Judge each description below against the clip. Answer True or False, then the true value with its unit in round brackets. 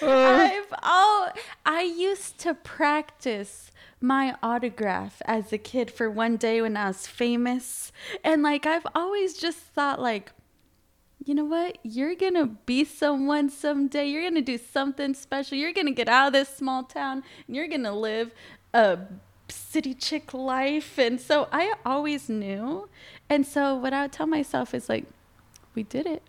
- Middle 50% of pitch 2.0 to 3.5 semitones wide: False (4.3 semitones)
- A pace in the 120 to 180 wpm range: True (170 wpm)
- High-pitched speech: True (275 Hz)